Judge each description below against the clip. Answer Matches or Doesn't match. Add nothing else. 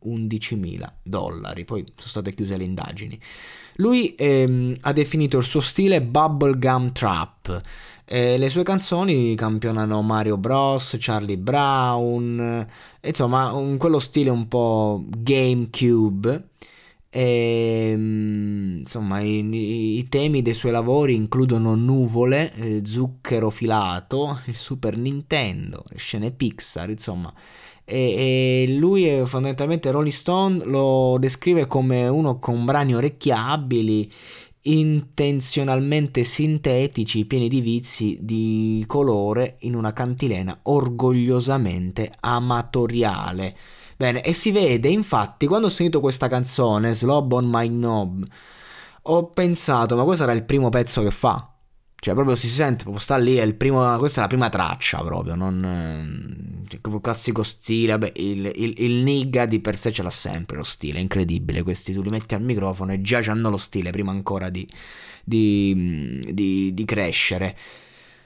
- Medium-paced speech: Matches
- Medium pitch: Doesn't match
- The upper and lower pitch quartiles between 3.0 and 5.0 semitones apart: Matches